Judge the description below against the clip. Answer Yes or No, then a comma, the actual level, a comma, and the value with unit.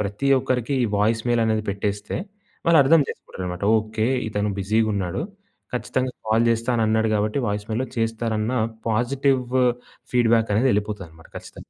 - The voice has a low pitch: Yes, low, 110 Hz